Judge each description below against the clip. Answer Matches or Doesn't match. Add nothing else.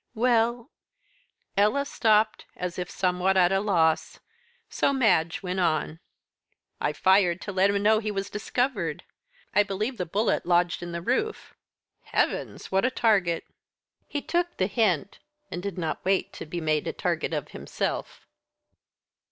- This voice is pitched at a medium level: Doesn't match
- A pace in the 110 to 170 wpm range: Matches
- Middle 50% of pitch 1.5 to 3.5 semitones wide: Doesn't match